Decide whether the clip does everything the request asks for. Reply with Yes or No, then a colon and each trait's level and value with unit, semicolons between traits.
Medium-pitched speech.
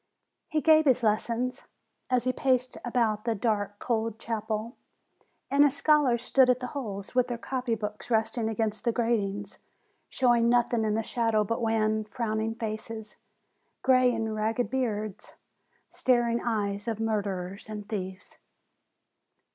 No: high, 225 Hz